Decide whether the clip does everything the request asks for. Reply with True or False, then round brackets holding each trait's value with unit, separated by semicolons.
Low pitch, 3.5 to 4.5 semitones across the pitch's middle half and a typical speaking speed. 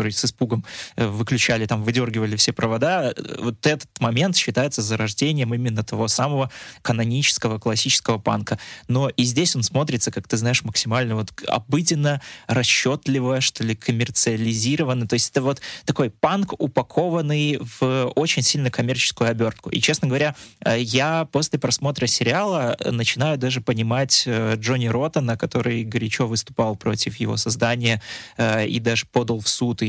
False (120 Hz; 3.0 semitones; 140 wpm)